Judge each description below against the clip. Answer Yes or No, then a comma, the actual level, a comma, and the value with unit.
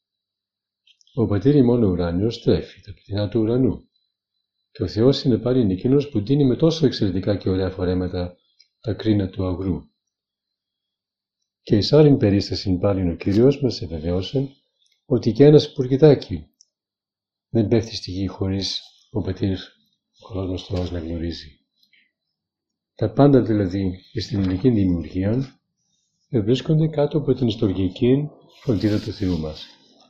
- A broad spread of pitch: No, average, 5.0 semitones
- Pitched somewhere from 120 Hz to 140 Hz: No, low, 100 Hz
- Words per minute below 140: Yes, average, 130 wpm